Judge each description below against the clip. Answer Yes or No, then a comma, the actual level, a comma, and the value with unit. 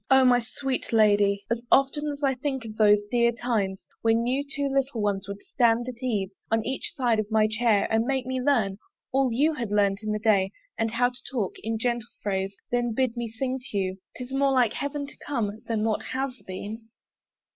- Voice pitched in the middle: No, high, 235 Hz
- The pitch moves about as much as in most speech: Yes, average, 3.6 semitones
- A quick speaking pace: Yes, fast, 210 wpm